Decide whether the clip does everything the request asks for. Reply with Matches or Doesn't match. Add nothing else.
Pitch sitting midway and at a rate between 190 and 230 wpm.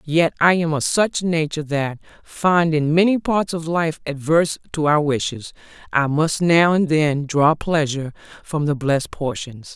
Doesn't match